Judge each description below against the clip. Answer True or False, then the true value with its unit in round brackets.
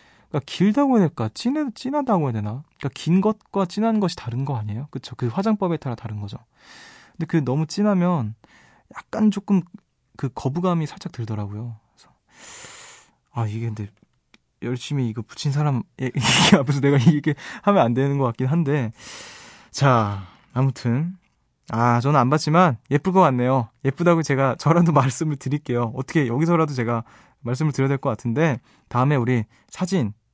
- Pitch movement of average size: False (6.2 semitones)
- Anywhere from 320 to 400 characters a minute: True (330 characters per minute)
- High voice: False (140 Hz)